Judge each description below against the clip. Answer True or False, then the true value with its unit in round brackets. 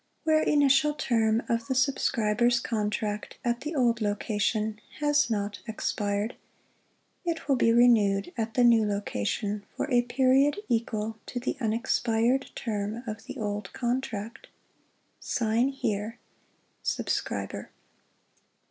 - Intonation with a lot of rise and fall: False (3.4 semitones)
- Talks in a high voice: True (230 Hz)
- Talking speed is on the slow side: True (120 wpm)